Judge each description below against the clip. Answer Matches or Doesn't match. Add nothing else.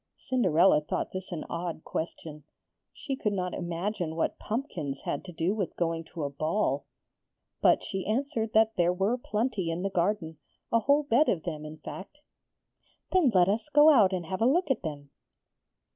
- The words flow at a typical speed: Matches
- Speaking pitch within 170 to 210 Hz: Matches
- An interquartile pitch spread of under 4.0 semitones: Doesn't match